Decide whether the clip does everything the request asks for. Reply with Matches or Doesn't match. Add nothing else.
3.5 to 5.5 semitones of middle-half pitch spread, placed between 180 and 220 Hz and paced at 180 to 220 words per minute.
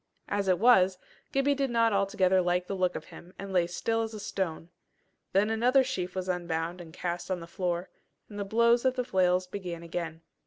Matches